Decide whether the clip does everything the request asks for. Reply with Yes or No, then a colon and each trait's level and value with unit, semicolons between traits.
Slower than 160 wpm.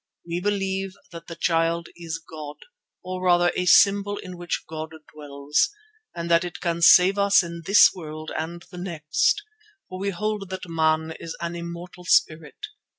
No: average, 165 wpm